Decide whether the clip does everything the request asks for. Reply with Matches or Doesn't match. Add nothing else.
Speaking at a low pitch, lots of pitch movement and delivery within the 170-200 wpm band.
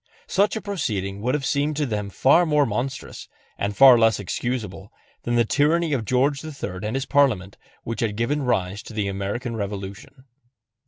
Matches